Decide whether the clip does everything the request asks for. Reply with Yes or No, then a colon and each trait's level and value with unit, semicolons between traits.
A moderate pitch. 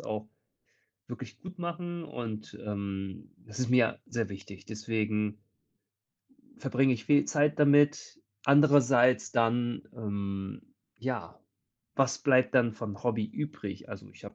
No: low, 120 Hz